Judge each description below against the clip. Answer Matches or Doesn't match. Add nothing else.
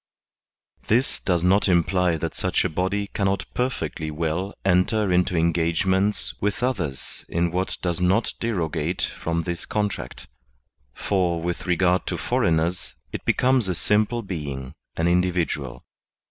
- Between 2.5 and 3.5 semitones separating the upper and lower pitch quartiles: Matches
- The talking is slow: Matches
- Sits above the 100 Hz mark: Doesn't match